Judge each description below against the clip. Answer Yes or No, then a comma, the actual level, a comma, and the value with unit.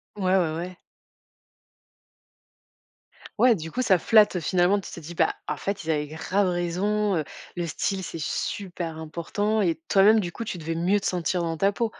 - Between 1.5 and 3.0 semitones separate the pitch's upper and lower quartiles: No, average, 3.5 semitones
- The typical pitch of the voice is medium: Yes, medium, 180 Hz